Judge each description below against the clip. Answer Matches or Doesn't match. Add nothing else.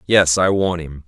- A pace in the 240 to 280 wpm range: Doesn't match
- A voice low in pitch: Matches